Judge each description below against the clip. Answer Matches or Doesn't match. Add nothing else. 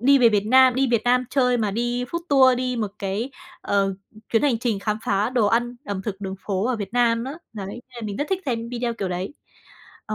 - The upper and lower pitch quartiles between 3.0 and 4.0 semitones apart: Matches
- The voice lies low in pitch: Doesn't match